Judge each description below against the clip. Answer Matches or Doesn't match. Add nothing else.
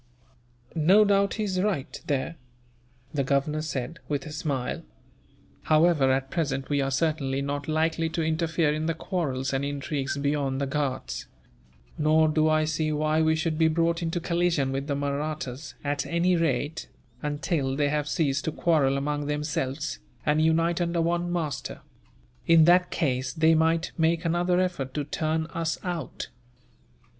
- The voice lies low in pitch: Doesn't match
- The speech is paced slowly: Doesn't match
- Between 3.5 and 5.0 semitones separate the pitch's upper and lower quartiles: Doesn't match